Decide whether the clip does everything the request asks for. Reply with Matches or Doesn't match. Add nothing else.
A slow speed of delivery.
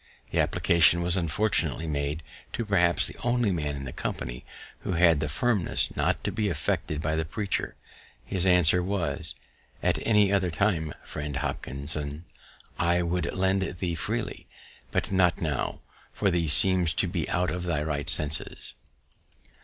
Doesn't match